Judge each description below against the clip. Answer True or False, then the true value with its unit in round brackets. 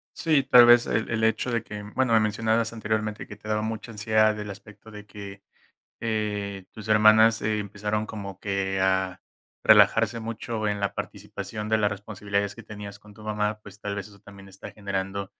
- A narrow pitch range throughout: True (1.5 semitones)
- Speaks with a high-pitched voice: False (105 Hz)